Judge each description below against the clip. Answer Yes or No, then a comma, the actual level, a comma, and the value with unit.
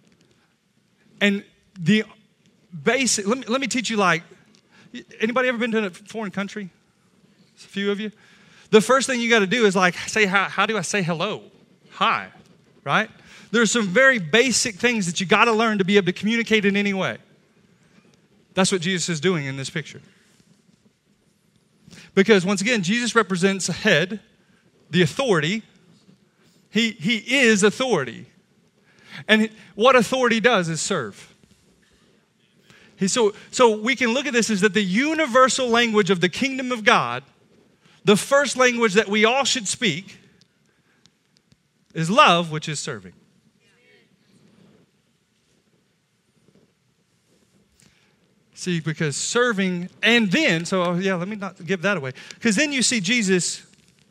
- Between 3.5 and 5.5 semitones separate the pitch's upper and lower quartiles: No, average, 2.8 semitones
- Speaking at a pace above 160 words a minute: No, average, 145 wpm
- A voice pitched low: No, high, 200 Hz